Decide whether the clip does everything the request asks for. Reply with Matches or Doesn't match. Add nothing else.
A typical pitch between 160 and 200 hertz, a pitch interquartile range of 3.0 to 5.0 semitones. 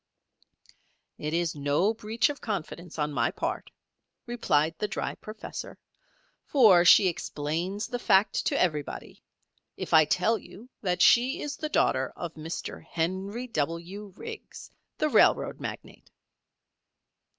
Doesn't match